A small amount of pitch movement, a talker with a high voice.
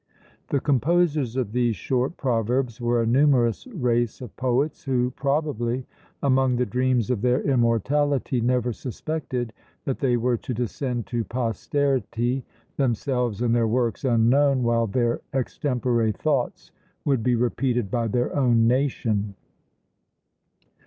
No: narrow, 2.3 semitones; low, 125 Hz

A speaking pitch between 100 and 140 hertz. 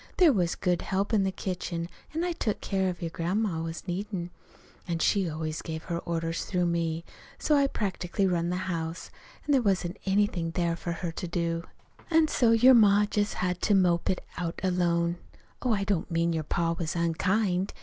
No: medium, 180 Hz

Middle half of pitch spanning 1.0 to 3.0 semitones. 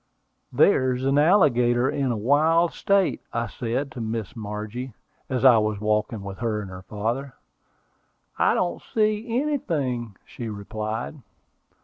No: average, 5.0 semitones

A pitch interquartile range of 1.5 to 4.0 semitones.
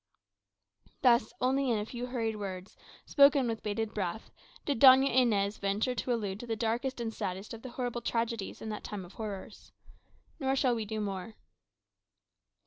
Yes: average, 3.1 semitones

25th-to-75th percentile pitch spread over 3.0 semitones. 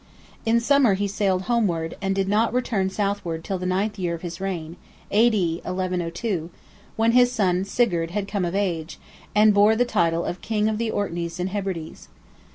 Yes: average, 3.7 semitones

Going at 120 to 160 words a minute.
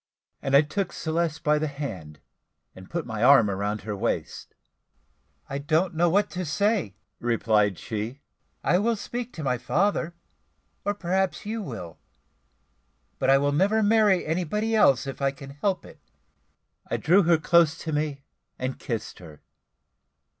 Yes: average, 155 wpm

